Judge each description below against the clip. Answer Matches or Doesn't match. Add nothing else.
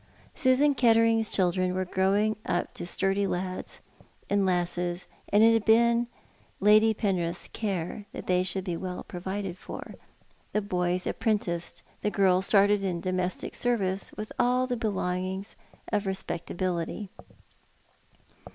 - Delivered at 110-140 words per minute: Matches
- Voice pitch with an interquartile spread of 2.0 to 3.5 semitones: Matches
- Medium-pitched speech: Doesn't match